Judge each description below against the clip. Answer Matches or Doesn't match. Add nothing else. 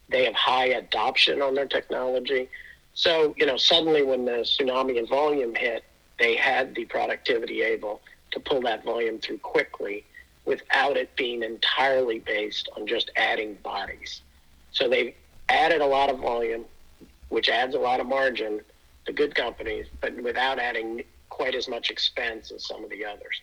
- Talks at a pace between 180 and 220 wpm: Doesn't match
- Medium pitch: Matches